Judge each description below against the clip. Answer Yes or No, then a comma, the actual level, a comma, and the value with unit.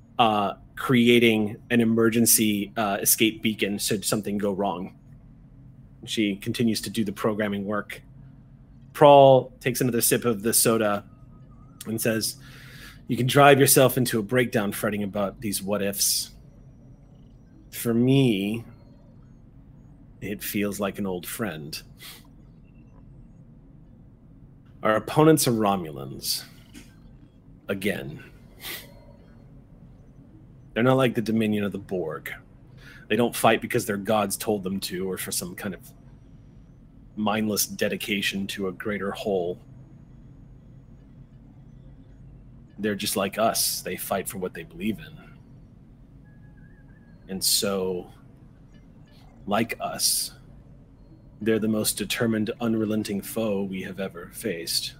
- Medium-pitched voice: No, low, 120 Hz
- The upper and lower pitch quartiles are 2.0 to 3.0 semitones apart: No, average, 3.8 semitones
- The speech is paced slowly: Yes, slow, 115 wpm